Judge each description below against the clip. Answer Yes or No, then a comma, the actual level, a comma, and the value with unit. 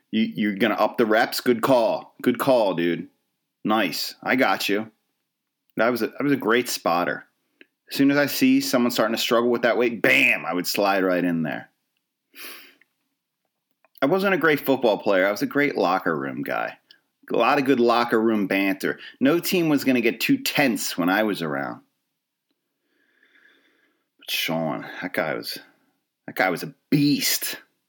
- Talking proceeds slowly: No, average, 180 wpm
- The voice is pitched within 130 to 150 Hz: Yes, medium, 140 Hz